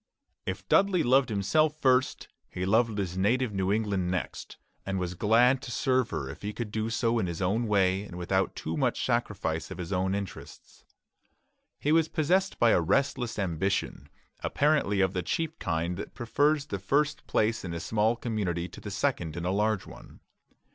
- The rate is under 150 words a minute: No, average, 185 wpm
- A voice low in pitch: Yes, low, 105 Hz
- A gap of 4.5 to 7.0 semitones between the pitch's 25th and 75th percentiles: Yes, wide, 5.4 semitones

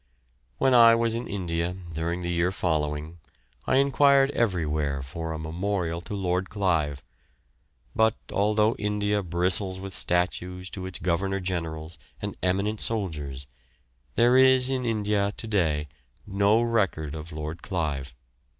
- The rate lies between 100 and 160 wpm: Yes, slow, 135 wpm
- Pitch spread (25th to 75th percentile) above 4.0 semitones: Yes, average, 4.4 semitones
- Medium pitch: No, very low, 95 Hz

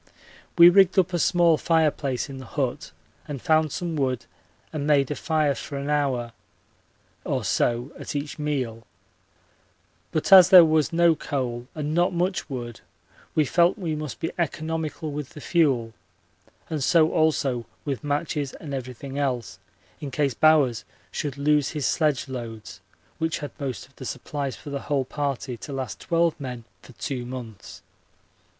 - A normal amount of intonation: Yes, average, 3.5 semitones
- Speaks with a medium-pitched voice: Yes, medium, 145 Hz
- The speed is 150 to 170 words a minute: Yes, average, 160 wpm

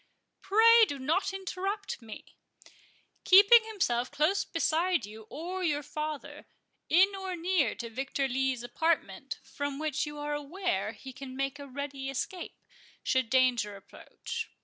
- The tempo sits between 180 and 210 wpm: No, slow, 135 wpm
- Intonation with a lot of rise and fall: Yes, wide, 6.0 semitones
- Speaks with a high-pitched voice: Yes, very high, 295 Hz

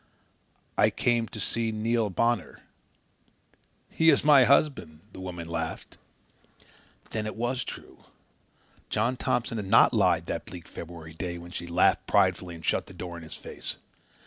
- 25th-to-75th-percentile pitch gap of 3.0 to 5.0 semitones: No, wide, 5.6 semitones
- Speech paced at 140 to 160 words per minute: Yes, average, 155 wpm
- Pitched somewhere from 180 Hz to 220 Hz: No, low, 105 Hz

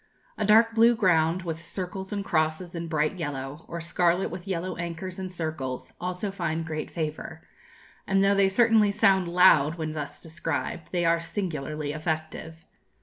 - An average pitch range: Yes, average, 3.3 semitones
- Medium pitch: Yes, medium, 170 Hz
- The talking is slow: No, average, 160 wpm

